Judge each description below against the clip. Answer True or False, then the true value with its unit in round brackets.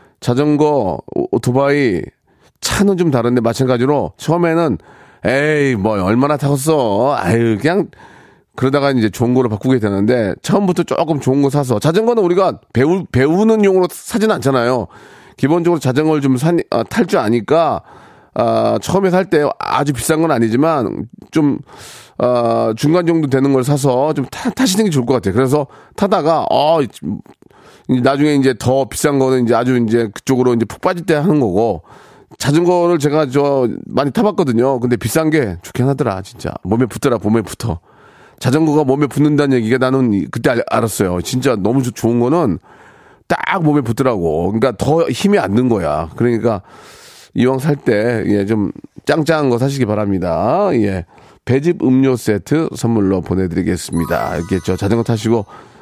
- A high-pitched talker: False (130 Hz)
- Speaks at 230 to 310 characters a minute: False (330 characters per minute)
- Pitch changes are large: False (4.6 semitones)